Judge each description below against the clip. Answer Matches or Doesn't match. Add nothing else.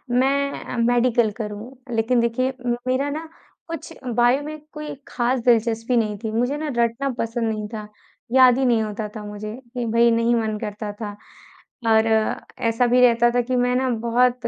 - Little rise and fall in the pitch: Matches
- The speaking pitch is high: Matches